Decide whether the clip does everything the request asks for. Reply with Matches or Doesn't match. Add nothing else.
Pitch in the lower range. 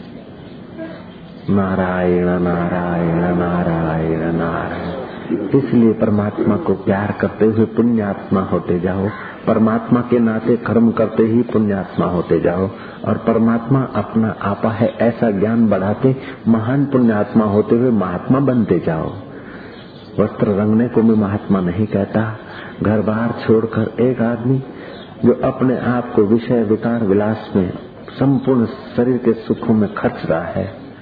Matches